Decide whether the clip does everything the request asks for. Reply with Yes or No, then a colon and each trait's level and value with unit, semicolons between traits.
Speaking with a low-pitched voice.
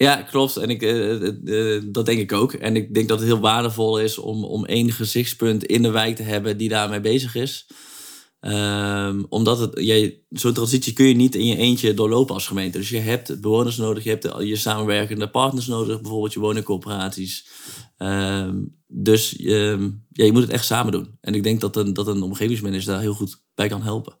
Yes: low, 110 Hz